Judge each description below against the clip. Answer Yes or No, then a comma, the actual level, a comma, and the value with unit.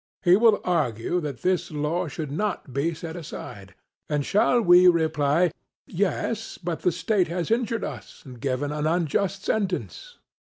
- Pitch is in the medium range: Yes, medium, 170 Hz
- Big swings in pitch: No, average, 4.5 semitones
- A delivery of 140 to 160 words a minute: Yes, average, 155 wpm